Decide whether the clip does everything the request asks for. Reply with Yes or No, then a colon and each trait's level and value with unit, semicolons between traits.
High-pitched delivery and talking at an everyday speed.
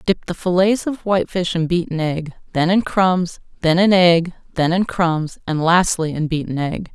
No: medium, 175 Hz; average, 190 wpm